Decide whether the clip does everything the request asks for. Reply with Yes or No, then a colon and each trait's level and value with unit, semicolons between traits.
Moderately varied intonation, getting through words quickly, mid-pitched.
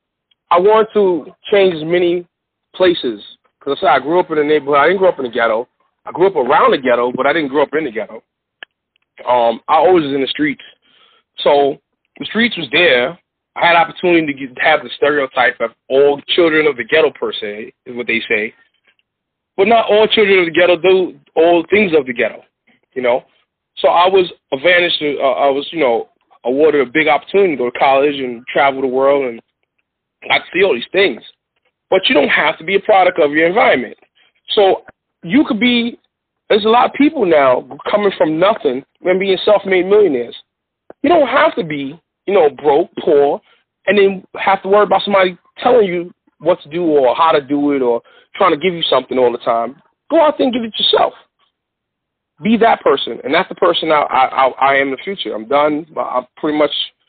No: wide, 6.6 semitones; fast, 210 wpm; medium, 175 Hz